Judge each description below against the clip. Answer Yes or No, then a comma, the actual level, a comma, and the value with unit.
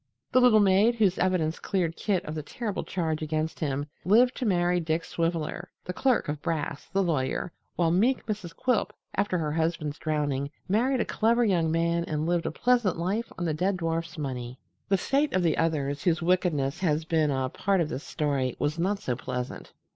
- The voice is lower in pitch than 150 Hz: No, medium, 170 Hz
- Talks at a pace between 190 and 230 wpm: Yes, average, 195 wpm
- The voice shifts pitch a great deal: No, average, 4.2 semitones